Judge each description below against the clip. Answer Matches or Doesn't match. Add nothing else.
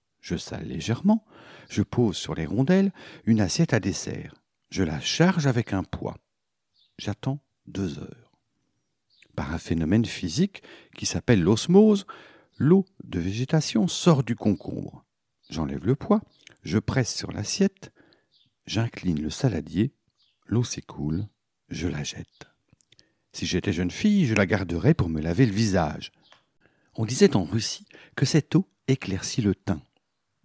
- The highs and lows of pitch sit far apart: Matches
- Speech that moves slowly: Matches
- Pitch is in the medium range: Doesn't match